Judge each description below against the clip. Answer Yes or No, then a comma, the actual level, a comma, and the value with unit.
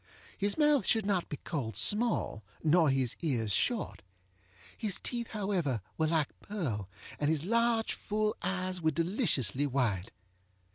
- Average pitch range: No, wide, 7.8 semitones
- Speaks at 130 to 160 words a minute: Yes, average, 140 wpm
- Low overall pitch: No, medium, 170 Hz